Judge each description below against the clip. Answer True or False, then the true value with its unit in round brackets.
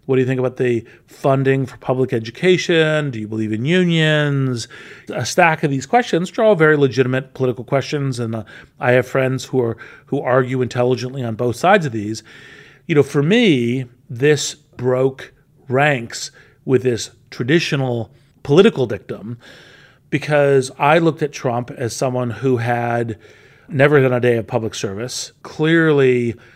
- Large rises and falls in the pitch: False (3.2 semitones)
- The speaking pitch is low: True (130 Hz)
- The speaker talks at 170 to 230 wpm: False (155 wpm)